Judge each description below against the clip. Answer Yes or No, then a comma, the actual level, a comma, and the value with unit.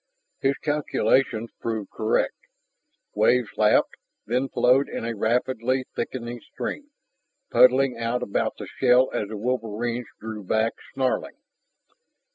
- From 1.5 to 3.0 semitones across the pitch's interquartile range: Yes, narrow, 2.6 semitones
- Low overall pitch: Yes, low, 120 Hz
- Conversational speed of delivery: No, slow, 115 wpm